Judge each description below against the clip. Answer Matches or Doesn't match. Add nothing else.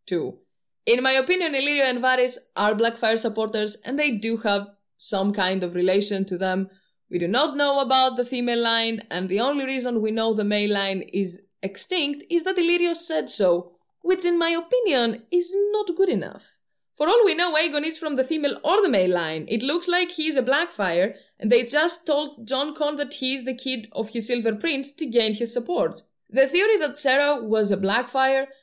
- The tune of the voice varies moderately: Doesn't match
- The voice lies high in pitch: Matches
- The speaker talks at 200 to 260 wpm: Matches